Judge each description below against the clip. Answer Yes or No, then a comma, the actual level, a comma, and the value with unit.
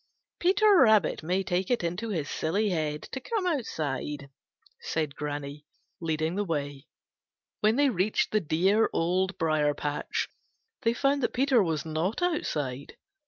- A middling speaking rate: Yes, average, 145 wpm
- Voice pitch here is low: No, medium, 175 Hz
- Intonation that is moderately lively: No, wide, 6.8 semitones